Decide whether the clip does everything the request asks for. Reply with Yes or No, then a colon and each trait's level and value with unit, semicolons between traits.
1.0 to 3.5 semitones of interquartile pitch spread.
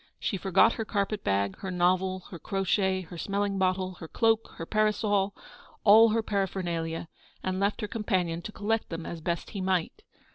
Yes: average, 2.9 semitones